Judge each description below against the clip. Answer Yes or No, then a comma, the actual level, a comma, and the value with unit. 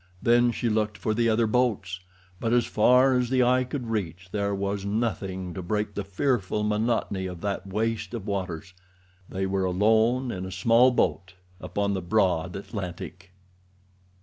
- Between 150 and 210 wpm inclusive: Yes, average, 160 wpm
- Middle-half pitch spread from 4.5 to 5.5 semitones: No, average, 3.6 semitones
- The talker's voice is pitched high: No, low, 100 Hz